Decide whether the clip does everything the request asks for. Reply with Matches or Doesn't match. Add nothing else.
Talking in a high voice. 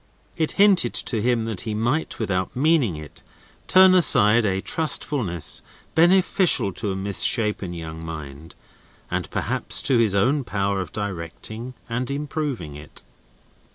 Doesn't match